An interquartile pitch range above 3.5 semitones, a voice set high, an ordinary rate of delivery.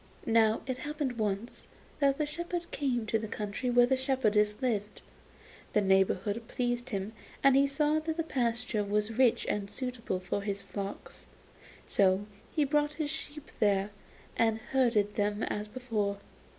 Yes: average, 4.5 semitones; high, 230 Hz; average, 155 wpm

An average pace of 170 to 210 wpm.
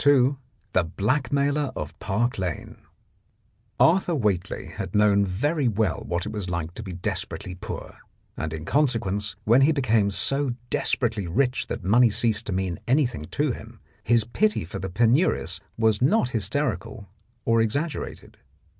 No: average, 150 wpm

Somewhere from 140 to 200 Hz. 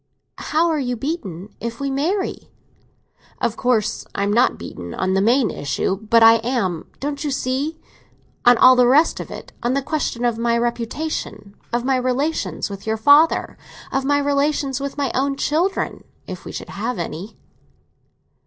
No: very high, 250 Hz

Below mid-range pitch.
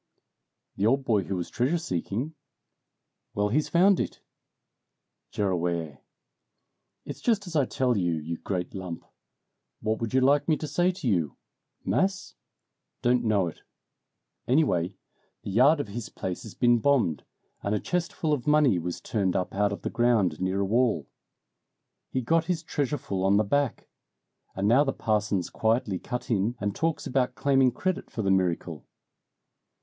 Yes: low, 115 Hz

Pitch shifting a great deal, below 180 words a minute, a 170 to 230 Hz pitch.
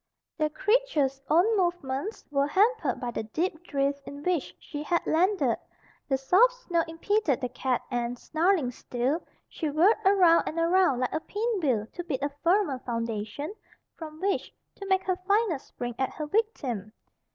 No: wide, 6.1 semitones; average, 165 wpm; very high, 315 Hz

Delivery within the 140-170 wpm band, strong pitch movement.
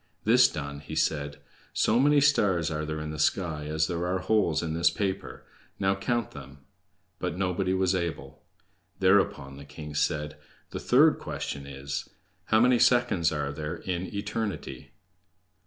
No: average, 155 wpm; average, 4.6 semitones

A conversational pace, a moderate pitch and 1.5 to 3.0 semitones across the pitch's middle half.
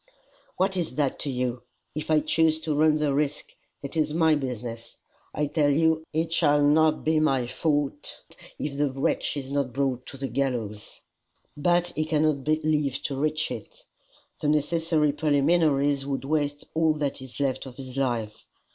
Yes: average, 170 wpm; medium, 145 Hz; narrow, 2.4 semitones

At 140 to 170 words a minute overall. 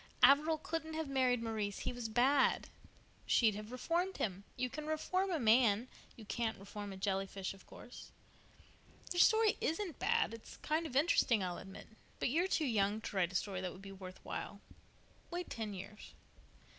No: average, 180 wpm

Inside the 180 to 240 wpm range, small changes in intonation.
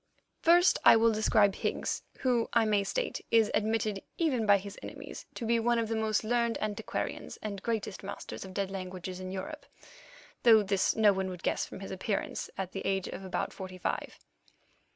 No: average, 190 wpm; average, 3.0 semitones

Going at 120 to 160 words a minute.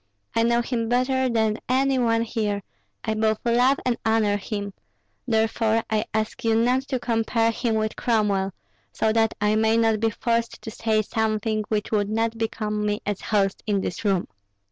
No: average, 180 wpm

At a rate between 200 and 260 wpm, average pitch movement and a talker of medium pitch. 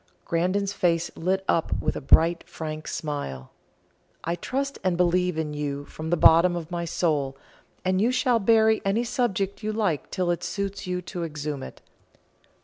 No: average, 170 wpm; average, 3.8 semitones; medium, 175 Hz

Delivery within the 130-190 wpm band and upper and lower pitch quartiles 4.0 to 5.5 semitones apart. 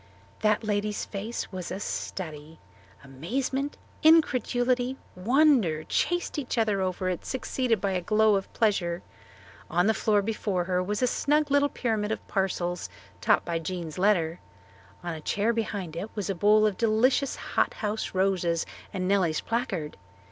Yes: average, 155 wpm; average, 4.4 semitones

